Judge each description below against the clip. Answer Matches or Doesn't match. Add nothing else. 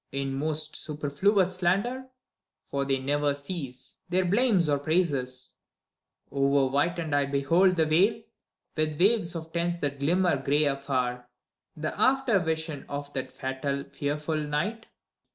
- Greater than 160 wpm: Doesn't match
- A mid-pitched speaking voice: Matches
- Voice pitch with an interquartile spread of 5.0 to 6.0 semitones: Doesn't match